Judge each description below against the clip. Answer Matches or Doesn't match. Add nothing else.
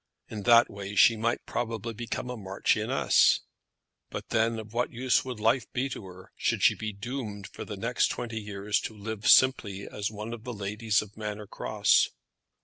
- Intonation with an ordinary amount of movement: Doesn't match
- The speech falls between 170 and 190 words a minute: Matches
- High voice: Doesn't match